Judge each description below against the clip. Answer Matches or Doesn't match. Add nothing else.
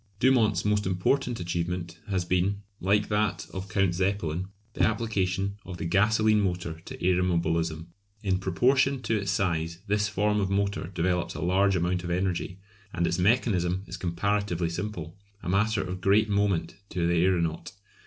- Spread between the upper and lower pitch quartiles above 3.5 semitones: Doesn't match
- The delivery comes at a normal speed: Matches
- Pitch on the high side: Doesn't match